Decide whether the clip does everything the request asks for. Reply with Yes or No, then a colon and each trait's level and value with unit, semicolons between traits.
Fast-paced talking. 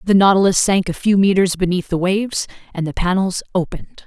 No: average, 190 wpm